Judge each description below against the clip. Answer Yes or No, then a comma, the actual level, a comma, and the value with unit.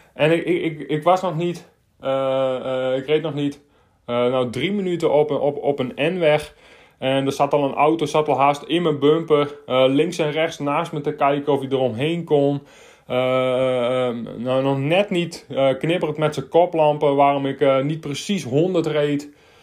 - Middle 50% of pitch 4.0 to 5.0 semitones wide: No, average, 2.7 semitones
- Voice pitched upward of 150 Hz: No, medium, 145 Hz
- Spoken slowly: No, fast, 200 wpm